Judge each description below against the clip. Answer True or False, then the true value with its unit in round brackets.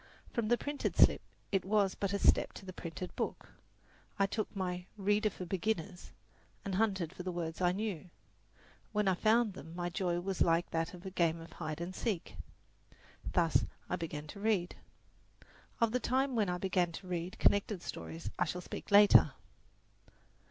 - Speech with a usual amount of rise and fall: True (3.0 semitones)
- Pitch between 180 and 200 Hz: True (185 Hz)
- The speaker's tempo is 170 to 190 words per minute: True (180 wpm)